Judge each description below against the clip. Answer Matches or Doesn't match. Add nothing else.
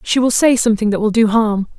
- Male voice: Doesn't match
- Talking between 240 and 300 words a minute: Matches